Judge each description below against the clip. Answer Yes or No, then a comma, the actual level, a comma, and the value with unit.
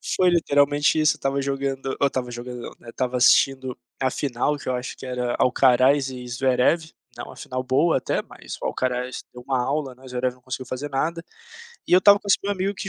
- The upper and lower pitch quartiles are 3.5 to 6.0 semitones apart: No, narrow, 2.5 semitones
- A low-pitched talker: Yes, low, 130 Hz